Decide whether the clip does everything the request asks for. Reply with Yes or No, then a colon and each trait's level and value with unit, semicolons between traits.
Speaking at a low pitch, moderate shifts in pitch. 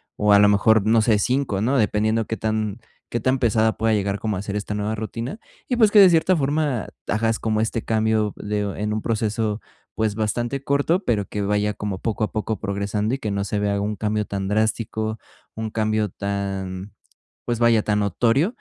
No: low, 110 Hz; narrow, 1.8 semitones